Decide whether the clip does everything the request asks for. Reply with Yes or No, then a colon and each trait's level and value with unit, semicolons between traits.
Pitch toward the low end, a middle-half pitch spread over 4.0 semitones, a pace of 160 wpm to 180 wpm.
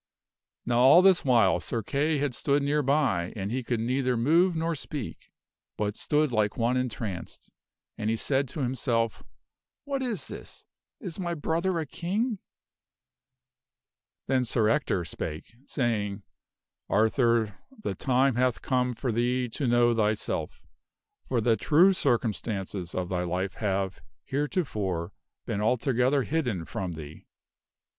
No: low, 125 Hz; average, 5.3 semitones; average, 140 wpm